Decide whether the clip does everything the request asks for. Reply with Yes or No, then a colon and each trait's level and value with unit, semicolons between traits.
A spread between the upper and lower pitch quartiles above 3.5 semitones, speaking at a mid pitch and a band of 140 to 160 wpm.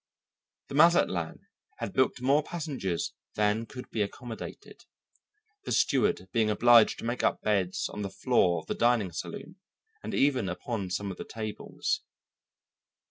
No: average, 4.7 semitones; low, 110 Hz; average, 145 wpm